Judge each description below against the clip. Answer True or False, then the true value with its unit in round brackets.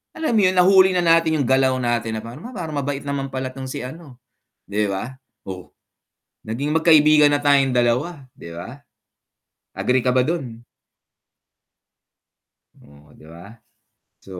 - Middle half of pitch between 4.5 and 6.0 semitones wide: True (5.1 semitones)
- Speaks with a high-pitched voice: False (135 Hz)